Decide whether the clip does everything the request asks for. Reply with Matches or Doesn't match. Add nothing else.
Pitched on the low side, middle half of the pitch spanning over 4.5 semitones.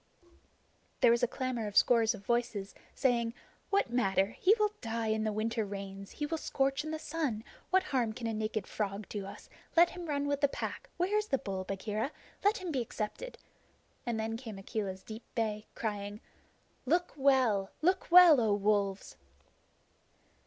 Doesn't match